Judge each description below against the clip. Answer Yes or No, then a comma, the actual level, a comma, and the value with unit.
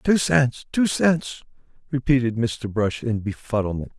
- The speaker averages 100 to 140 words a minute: Yes, slow, 135 wpm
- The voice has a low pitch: Yes, low, 120 Hz